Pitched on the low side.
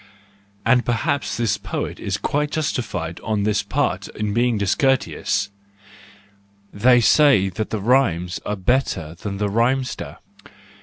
Yes: low, 110 Hz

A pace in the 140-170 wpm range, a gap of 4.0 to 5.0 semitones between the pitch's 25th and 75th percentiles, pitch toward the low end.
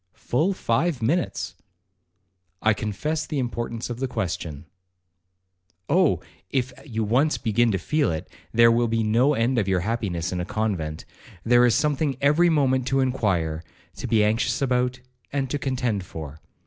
Yes: average, 160 wpm; average, 4.5 semitones; low, 120 Hz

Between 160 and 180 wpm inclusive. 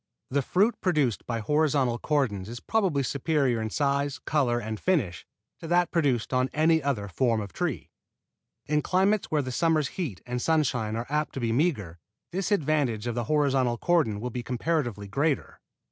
Yes: average, 175 wpm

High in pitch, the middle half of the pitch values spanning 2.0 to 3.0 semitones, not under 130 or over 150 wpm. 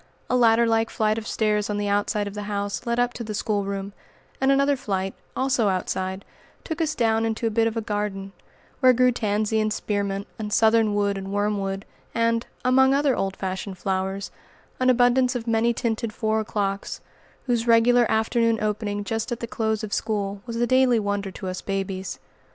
No: high, 220 Hz; narrow, 2.6 semitones; average, 185 wpm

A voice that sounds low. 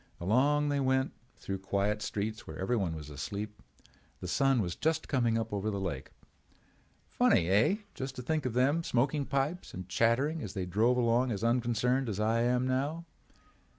Yes: low, 120 Hz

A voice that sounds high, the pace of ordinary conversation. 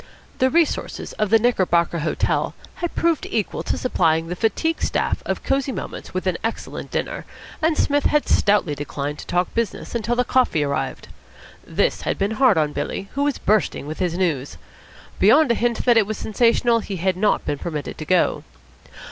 Yes: high, 210 Hz; average, 185 wpm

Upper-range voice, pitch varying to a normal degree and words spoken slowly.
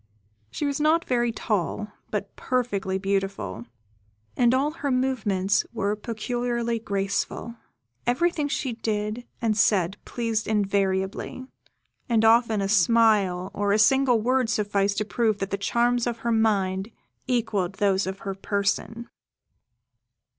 Yes: high, 215 Hz; average, 3.4 semitones; slow, 130 wpm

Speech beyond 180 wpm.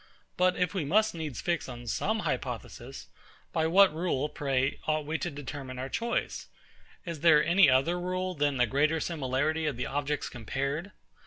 No: average, 170 wpm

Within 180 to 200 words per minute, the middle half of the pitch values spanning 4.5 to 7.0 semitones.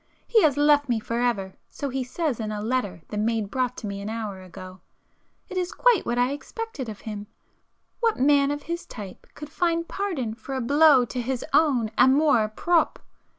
Yes: average, 195 wpm; wide, 5.5 semitones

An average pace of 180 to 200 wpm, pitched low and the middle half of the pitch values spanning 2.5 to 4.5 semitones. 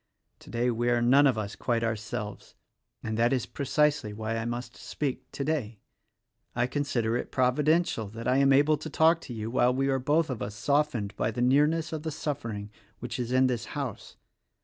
Yes: average, 195 wpm; low, 125 Hz; average, 4.0 semitones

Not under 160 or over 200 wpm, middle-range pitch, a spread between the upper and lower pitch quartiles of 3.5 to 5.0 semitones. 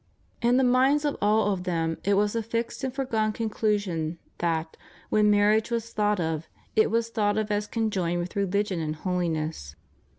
No: average, 185 wpm; high, 205 Hz; average, 4.5 semitones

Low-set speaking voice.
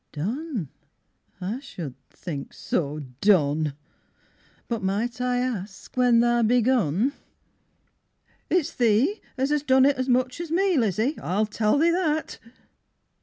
No: high, 240 Hz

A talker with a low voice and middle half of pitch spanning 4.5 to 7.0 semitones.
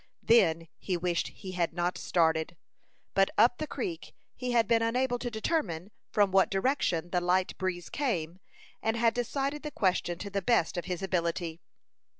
No: high, 195 Hz; average, 5.3 semitones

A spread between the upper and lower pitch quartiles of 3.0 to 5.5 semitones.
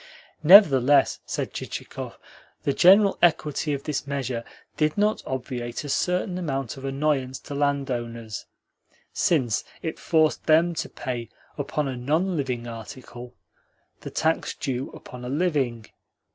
Yes: average, 4.0 semitones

